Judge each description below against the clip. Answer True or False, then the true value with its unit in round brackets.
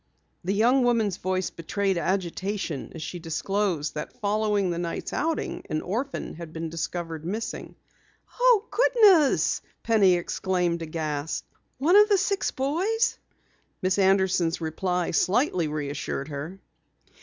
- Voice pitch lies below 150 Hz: False (185 Hz)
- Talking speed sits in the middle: False (125 wpm)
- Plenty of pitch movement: True (6.1 semitones)